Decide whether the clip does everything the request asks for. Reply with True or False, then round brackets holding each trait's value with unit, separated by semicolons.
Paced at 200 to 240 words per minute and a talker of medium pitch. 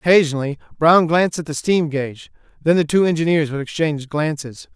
False (175 wpm; 155 Hz)